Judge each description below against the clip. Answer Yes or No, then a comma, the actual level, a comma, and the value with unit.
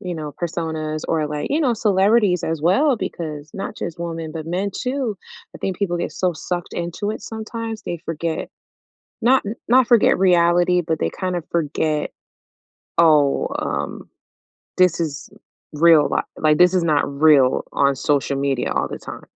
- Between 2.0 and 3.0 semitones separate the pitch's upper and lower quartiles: No, average, 3.9 semitones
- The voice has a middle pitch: Yes, medium, 170 Hz